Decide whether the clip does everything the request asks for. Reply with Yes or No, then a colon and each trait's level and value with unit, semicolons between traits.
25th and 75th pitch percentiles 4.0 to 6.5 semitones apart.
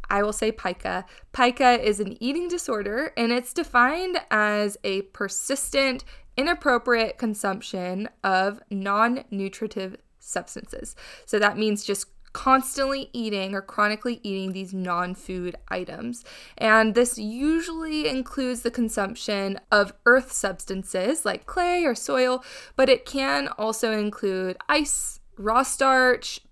Yes: average, 4.4 semitones